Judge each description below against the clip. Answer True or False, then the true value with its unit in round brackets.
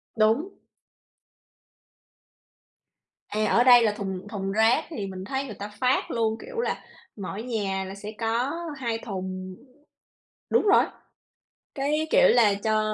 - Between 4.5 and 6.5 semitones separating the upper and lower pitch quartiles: False (4.0 semitones)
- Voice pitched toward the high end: True (220 Hz)